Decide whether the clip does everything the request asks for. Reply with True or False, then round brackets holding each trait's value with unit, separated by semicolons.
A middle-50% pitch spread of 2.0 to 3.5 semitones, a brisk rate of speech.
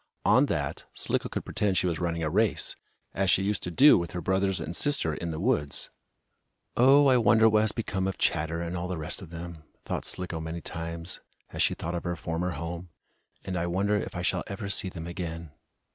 True (2.8 semitones; 220 wpm)